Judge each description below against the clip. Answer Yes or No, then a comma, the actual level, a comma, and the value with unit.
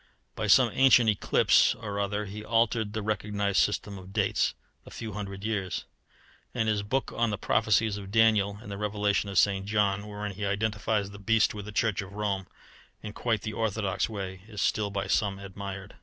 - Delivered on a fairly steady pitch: Yes, narrow, 1.5 semitones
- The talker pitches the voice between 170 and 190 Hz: No, low, 105 Hz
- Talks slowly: No, average, 190 wpm